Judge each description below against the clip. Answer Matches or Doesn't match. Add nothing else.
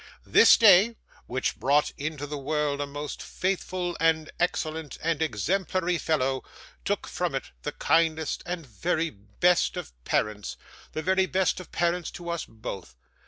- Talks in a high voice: Doesn't match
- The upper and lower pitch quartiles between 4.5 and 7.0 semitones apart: Doesn't match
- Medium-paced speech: Matches